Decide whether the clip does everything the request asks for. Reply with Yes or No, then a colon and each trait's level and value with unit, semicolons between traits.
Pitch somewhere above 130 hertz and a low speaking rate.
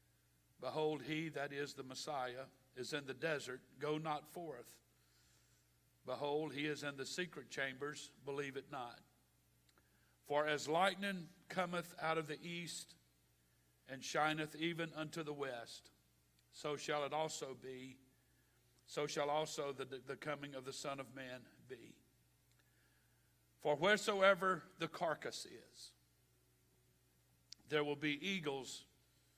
Yes: medium, 140 Hz; slow, 130 wpm